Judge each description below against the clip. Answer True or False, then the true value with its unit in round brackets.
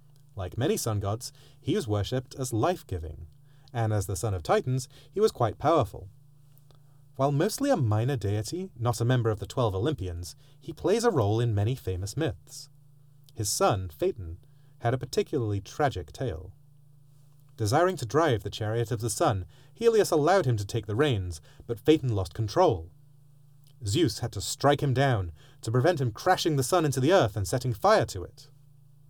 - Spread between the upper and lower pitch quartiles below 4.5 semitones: False (4.8 semitones)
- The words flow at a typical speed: True (180 wpm)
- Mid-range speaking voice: False (130 Hz)